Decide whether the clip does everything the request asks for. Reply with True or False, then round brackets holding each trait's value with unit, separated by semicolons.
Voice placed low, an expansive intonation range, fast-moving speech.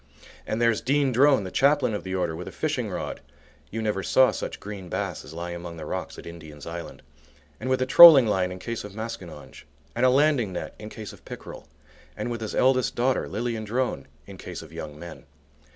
True (105 Hz; 6.4 semitones; 215 wpm)